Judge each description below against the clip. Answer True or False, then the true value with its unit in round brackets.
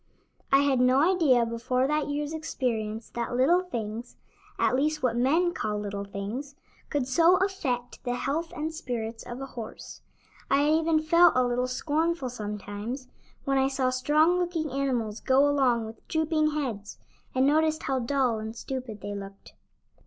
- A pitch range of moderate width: True (4.6 semitones)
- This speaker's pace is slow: False (165 wpm)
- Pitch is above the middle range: True (260 Hz)